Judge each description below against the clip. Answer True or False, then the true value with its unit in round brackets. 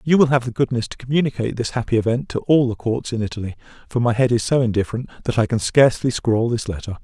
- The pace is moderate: False (245 wpm)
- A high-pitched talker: False (120 Hz)